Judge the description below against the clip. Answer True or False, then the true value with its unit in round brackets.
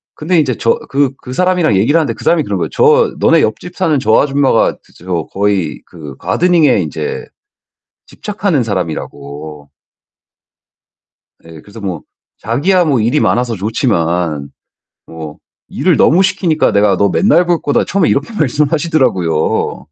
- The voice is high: False (125 Hz)